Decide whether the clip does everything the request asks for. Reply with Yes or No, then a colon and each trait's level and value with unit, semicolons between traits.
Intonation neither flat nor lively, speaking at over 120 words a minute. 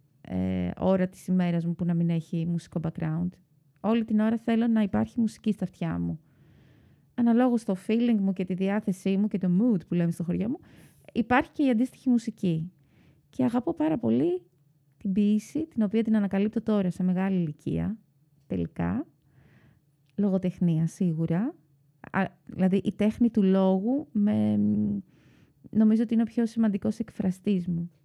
Yes: average, 4.8 semitones; average, 160 wpm